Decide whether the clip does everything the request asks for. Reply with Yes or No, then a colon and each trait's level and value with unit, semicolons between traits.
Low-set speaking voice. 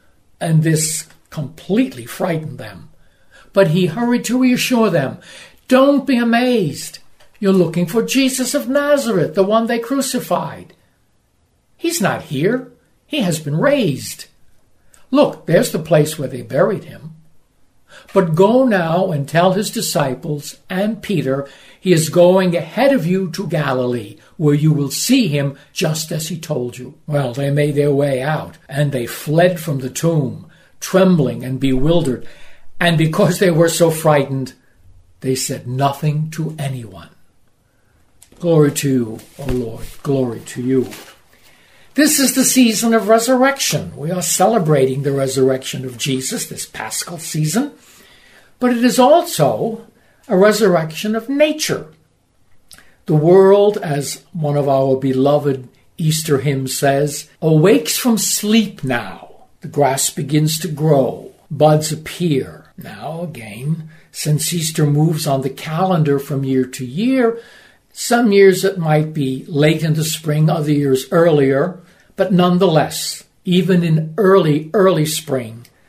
No: medium, 160 Hz